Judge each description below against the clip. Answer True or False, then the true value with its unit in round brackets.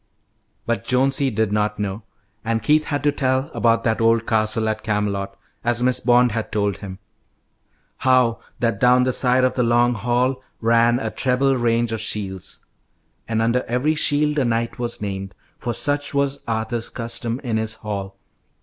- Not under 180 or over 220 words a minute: False (170 wpm)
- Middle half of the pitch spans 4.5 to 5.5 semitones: False (2.5 semitones)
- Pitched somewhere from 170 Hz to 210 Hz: False (115 Hz)